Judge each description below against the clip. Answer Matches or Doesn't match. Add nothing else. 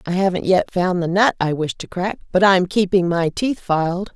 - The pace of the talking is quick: Matches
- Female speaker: Matches